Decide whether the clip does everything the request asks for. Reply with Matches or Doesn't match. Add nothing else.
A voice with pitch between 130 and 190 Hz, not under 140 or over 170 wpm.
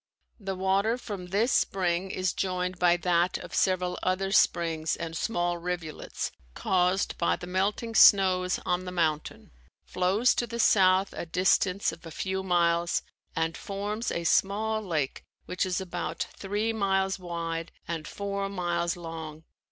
Matches